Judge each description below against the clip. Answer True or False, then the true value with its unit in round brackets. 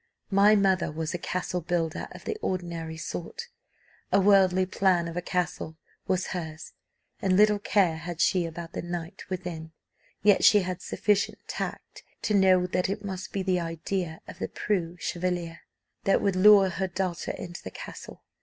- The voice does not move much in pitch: True (2.3 semitones)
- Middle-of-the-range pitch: True (180 Hz)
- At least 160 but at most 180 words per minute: True (170 wpm)